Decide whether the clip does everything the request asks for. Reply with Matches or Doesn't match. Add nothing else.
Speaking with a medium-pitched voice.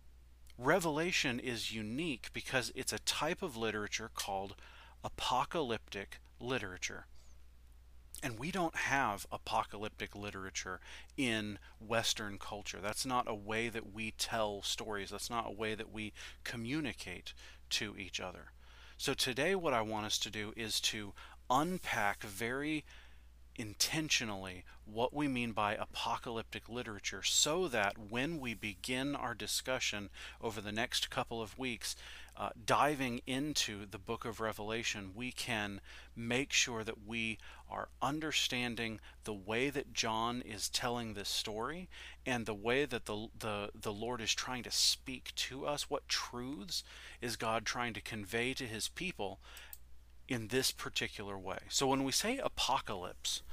Doesn't match